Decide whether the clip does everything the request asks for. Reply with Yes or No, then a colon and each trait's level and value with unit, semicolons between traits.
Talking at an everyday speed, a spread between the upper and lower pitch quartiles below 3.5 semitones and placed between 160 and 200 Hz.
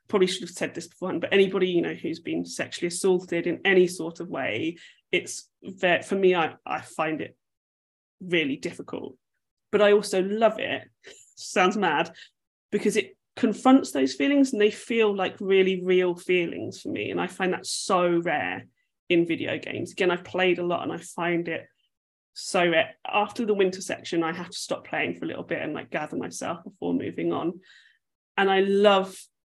Yes: average, 190 wpm; average, 3.0 semitones; high, 190 Hz